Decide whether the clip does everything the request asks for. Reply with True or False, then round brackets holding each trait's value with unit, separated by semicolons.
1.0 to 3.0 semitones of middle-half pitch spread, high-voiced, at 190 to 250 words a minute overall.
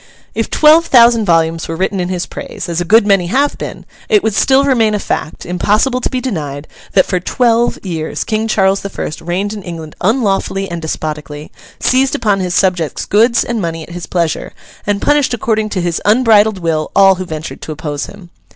False (4.9 semitones; 195 Hz; 200 wpm)